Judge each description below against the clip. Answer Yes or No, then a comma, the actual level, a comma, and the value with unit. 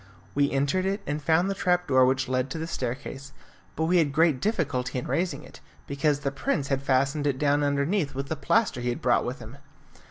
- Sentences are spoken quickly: Yes, fast, 220 wpm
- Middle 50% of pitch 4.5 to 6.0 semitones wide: No, average, 3.4 semitones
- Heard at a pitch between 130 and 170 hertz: Yes, medium, 140 Hz